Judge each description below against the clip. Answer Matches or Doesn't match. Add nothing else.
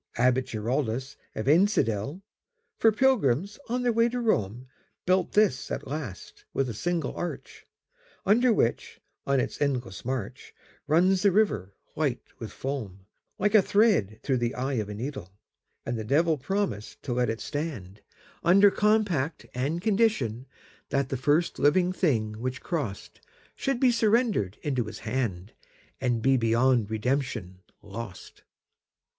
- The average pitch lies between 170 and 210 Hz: Doesn't match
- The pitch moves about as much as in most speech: Doesn't match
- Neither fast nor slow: Doesn't match